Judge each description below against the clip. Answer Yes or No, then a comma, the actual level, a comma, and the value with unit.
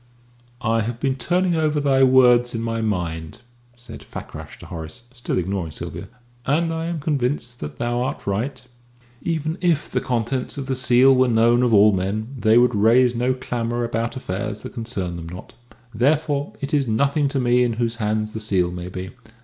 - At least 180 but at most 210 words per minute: Yes, average, 190 wpm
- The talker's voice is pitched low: Yes, low, 120 Hz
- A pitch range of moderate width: Yes, average, 3.7 semitones